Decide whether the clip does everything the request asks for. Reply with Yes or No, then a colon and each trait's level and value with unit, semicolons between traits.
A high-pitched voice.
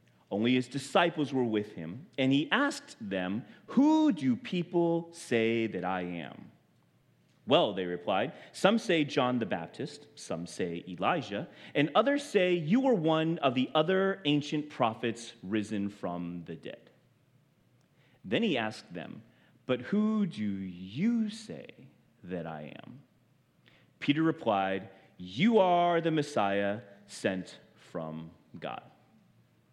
No: medium, 140 Hz